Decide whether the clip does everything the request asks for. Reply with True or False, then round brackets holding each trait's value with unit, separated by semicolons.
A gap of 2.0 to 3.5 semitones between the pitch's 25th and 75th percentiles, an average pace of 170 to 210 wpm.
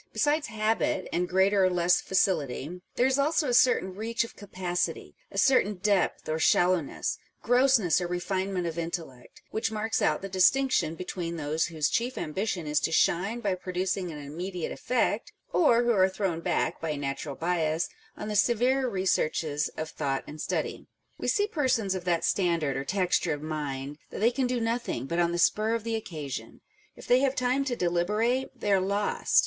False (5.6 semitones; 185 wpm)